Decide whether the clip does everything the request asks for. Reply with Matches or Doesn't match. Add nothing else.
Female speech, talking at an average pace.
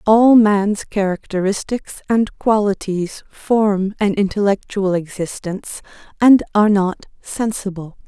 Doesn't match